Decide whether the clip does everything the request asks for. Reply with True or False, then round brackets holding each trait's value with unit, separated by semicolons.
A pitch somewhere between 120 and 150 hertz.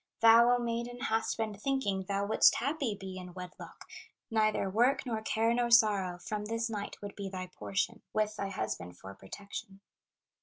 False (215 Hz)